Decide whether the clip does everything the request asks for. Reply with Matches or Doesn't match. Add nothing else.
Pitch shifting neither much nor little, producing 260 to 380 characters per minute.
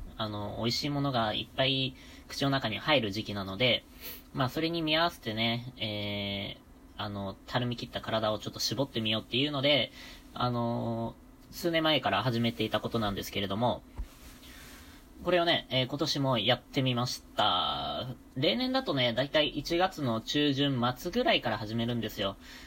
Matches